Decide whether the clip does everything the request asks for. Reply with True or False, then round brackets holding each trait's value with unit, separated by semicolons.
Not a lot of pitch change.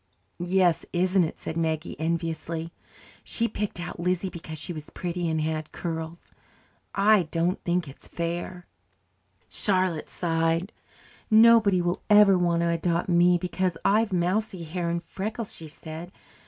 True (2.1 semitones)